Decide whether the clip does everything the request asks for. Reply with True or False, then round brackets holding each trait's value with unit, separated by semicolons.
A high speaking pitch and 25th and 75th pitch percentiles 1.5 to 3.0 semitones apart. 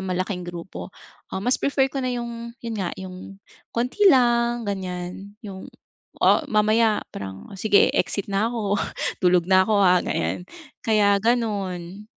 False (205 Hz; 4.0 semitones)